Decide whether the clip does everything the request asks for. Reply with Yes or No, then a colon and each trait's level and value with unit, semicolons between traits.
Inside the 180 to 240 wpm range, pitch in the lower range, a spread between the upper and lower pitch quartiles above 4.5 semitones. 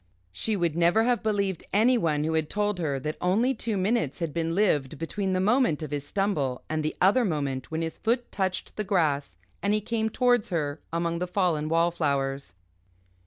No: average, 190 wpm; medium, 175 Hz; average, 5.3 semitones